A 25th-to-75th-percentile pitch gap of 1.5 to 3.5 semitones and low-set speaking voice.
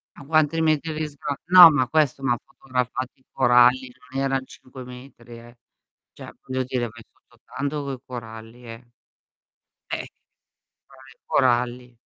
Yes: narrow, 2.6 semitones; low, 130 Hz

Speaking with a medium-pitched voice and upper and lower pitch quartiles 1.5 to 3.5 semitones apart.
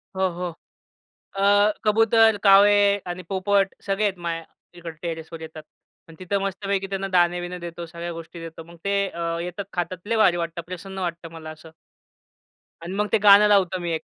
Yes: medium, 180 Hz; average, 2.9 semitones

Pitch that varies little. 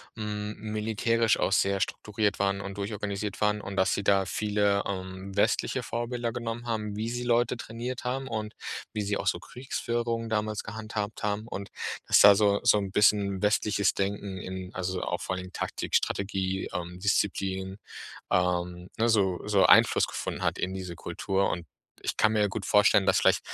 Yes: narrow, 2.2 semitones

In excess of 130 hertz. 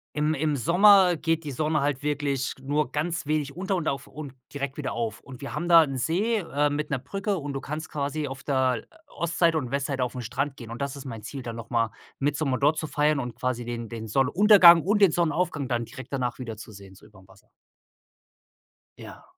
Yes: medium, 140 Hz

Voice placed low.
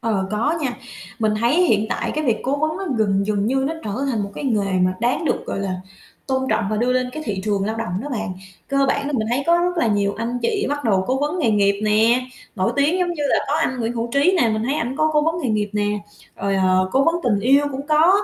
No: high, 240 Hz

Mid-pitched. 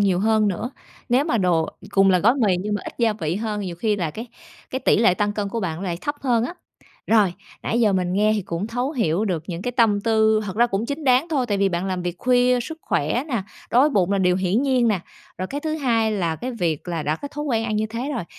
No: high, 215 Hz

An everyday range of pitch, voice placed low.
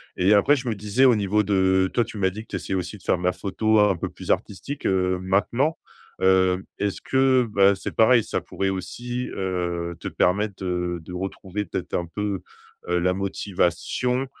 Yes: average, 3.0 semitones; very low, 95 Hz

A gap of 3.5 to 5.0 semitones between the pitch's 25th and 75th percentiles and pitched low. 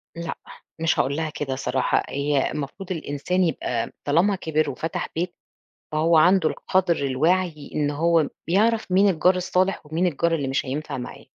No: average, 4.0 semitones; medium, 160 Hz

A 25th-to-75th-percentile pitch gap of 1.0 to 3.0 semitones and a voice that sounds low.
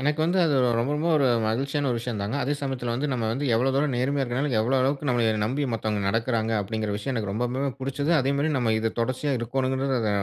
No: average, 3.5 semitones; low, 130 Hz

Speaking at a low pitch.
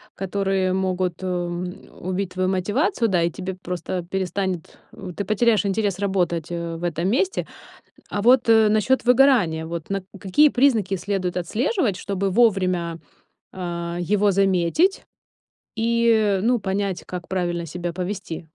No: high, 190 Hz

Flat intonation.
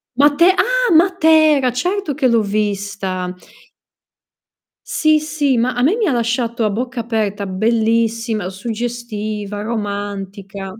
No: wide, 5.6 semitones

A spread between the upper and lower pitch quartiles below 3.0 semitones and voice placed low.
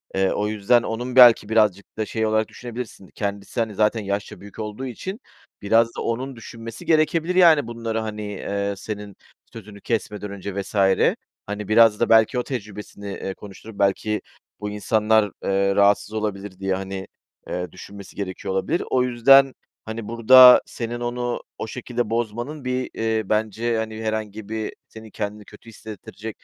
Yes: narrow, 2.4 semitones; low, 110 Hz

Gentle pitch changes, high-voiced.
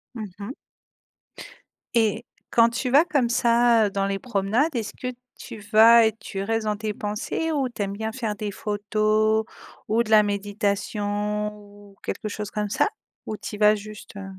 Yes: narrow, 1.9 semitones; high, 215 Hz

